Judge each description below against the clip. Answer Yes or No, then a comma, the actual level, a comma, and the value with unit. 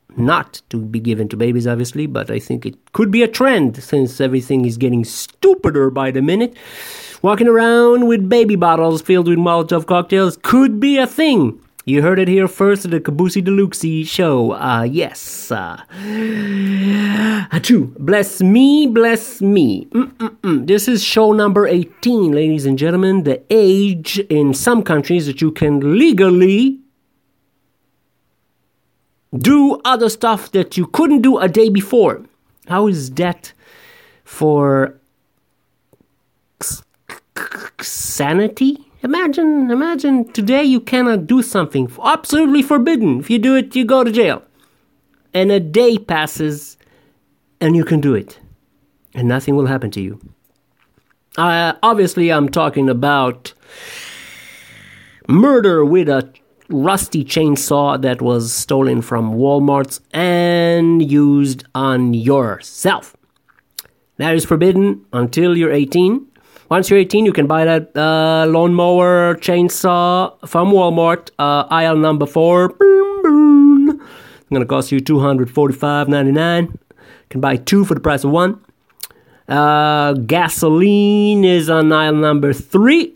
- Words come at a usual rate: No, slow, 130 wpm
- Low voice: No, medium, 175 Hz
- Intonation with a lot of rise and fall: Yes, wide, 7.6 semitones